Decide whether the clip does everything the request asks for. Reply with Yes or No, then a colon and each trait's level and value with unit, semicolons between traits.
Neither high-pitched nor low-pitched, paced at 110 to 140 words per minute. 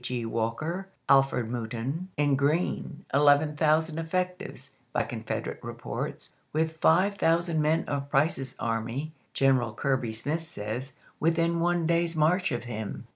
Yes: medium, 150 Hz; slow, 135 wpm